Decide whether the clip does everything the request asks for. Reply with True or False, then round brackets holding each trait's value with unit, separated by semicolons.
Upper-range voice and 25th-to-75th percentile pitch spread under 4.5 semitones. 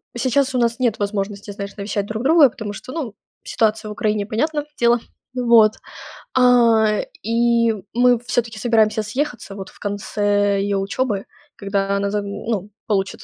True (215 Hz; 2.8 semitones)